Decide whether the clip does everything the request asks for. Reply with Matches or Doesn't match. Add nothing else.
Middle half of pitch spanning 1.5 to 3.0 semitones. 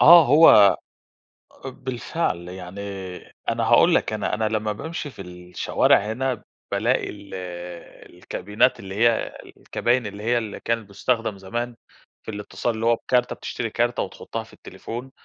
Doesn't match